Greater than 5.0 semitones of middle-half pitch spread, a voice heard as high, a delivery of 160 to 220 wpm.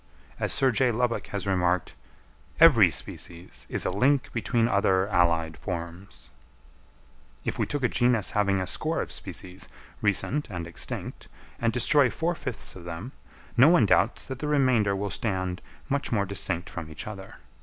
No: wide, 5.6 semitones; low, 100 Hz; average, 165 wpm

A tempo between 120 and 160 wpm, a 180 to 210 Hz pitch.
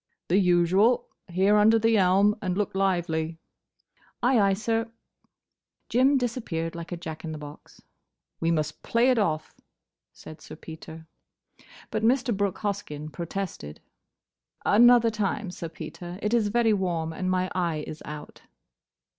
Yes: average, 145 wpm; medium, 185 Hz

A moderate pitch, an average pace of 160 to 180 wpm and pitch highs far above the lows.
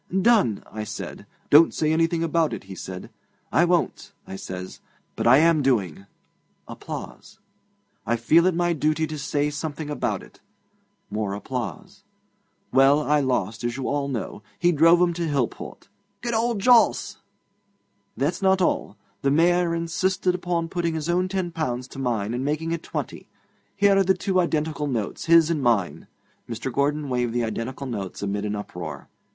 Yes: medium, 150 Hz; average, 170 wpm; wide, 6.2 semitones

